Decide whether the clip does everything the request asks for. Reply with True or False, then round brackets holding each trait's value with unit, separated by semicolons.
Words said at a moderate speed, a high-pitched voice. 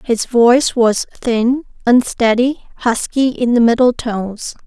False (130 wpm; 240 Hz)